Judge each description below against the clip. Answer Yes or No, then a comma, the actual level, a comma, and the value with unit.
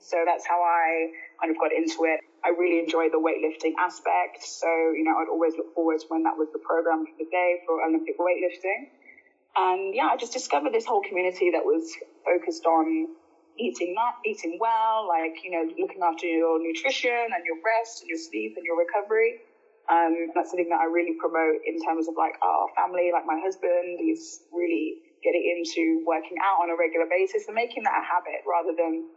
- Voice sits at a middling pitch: Yes, medium, 170 Hz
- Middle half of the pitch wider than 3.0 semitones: Yes, average, 5.3 semitones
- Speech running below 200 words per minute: No, fast, 205 wpm